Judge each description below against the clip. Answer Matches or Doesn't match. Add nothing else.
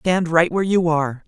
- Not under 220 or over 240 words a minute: Matches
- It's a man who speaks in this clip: Matches